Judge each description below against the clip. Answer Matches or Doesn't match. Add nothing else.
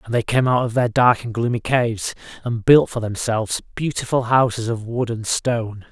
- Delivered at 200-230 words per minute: Matches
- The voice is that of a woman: Doesn't match